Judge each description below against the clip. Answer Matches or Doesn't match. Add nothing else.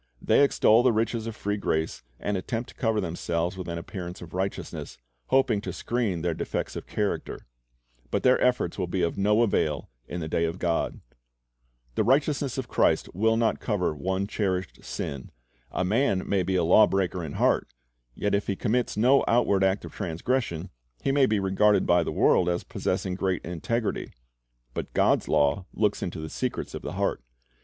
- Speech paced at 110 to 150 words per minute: Doesn't match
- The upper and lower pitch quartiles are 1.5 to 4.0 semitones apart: Doesn't match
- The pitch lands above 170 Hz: Doesn't match